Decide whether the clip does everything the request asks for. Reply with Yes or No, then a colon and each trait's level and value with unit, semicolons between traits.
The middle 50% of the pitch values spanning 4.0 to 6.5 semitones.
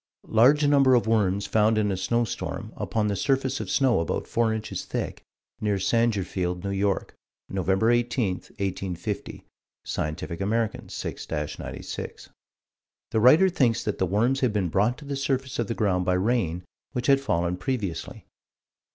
Yes: average, 4.5 semitones